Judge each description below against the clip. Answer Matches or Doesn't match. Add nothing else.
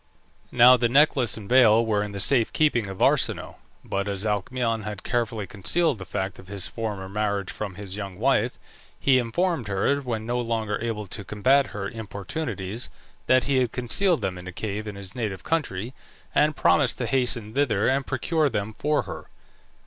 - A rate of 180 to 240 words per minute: Matches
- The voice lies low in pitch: Matches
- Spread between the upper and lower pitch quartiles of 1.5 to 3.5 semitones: Doesn't match